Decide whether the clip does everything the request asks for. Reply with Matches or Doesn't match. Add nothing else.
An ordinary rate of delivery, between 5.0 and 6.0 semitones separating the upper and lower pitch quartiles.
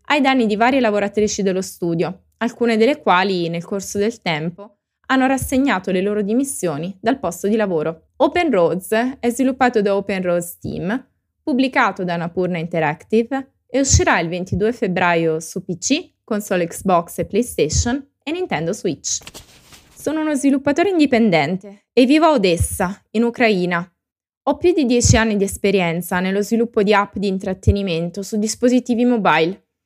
Matches